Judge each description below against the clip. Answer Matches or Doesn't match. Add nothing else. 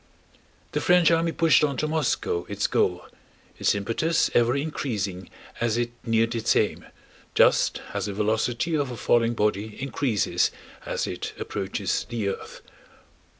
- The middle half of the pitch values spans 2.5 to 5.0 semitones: Doesn't match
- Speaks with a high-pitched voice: Doesn't match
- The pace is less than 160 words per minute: Matches